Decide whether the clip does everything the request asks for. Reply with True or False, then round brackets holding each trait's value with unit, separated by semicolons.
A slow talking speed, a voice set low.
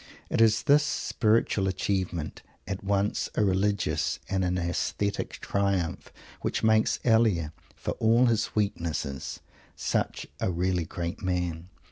True (125 wpm; 95 Hz)